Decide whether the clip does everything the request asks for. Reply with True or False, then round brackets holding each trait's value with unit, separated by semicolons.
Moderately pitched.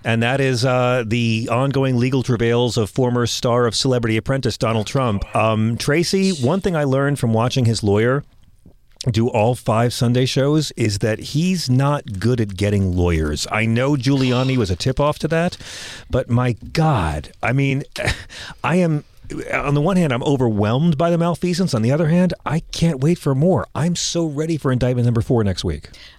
False (125 Hz)